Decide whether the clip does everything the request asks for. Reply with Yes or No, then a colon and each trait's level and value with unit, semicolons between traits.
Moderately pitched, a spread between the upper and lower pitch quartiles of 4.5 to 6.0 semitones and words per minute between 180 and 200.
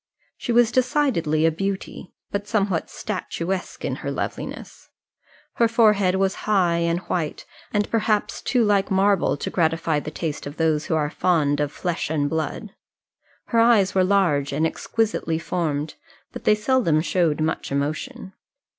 No: medium, 180 Hz; average, 4.8 semitones; average, 155 wpm